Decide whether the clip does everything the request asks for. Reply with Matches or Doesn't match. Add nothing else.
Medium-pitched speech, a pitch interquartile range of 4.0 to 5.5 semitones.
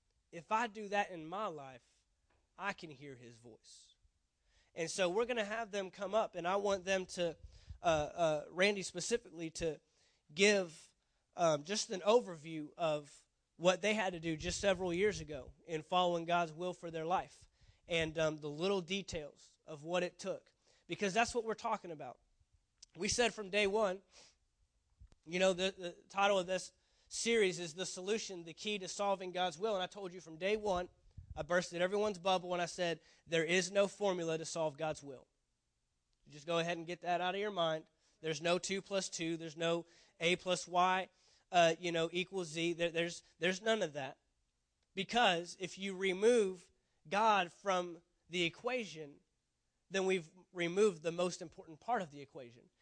Doesn't match